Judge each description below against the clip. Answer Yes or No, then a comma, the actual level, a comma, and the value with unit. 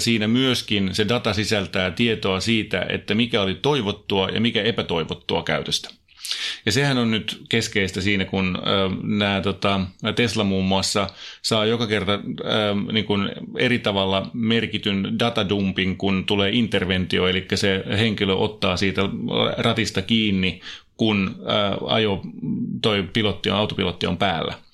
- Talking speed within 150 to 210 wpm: No, average, 135 wpm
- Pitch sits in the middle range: No, low, 105 Hz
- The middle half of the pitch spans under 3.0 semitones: Yes, narrow, 2.6 semitones